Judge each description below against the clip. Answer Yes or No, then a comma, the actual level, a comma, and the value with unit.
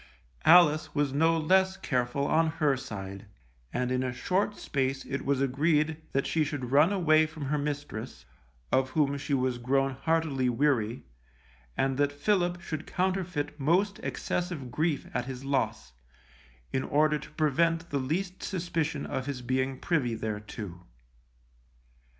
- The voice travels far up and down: No, average, 3.8 semitones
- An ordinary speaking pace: Yes, average, 145 wpm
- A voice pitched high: No, medium, 145 Hz